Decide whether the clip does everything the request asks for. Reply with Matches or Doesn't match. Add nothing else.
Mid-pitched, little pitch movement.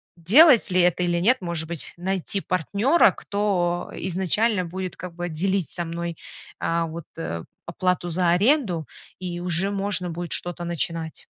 Matches